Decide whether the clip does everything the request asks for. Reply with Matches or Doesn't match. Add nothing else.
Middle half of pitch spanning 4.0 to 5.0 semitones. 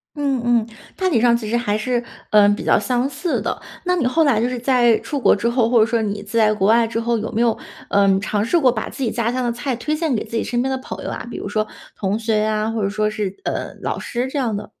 Doesn't match